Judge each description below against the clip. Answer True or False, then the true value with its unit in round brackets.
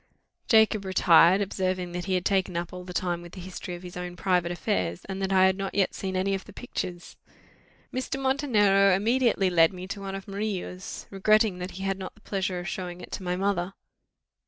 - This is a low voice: False (190 Hz)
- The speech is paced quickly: True (215 wpm)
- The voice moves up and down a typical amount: False (1.7 semitones)